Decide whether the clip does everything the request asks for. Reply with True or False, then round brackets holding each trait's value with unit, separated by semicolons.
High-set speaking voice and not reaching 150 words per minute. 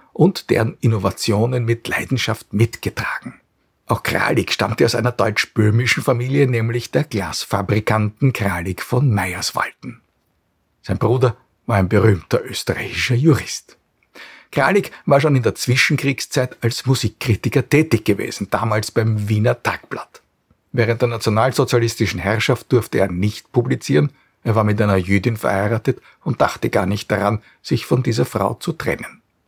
False (115 Hz; 130 wpm)